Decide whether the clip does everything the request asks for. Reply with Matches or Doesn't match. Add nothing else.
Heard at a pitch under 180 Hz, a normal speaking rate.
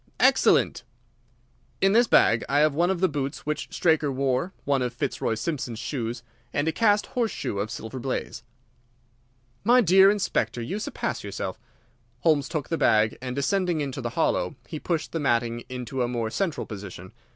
Matches